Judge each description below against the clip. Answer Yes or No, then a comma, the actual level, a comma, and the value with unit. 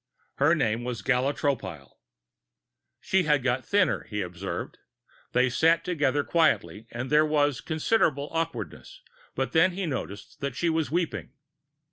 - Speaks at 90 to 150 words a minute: Yes, average, 140 wpm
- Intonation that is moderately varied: Yes, average, 5.0 semitones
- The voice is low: No, medium, 145 Hz